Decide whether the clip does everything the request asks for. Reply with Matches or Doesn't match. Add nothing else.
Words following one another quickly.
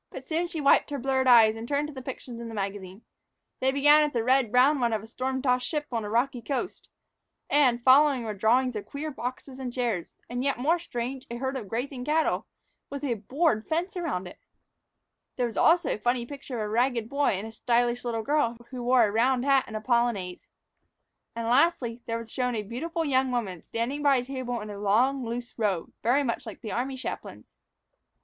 Matches